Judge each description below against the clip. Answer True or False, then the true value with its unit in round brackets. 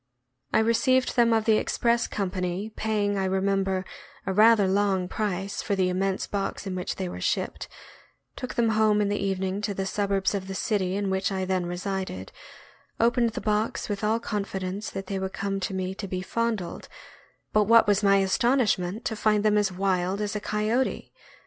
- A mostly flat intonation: True (2.1 semitones)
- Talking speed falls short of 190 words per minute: False (195 wpm)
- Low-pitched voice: False (200 Hz)